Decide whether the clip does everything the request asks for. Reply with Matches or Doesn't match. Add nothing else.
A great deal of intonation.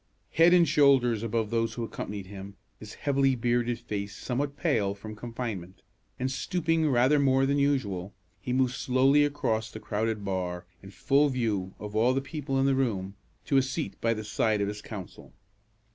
Doesn't match